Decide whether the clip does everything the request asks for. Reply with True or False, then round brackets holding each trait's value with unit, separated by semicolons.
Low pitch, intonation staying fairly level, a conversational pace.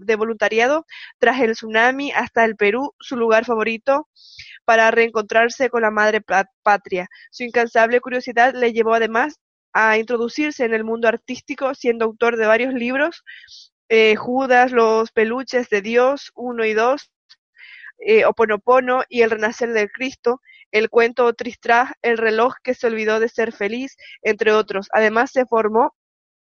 False (235 Hz; 2.2 semitones; 150 wpm)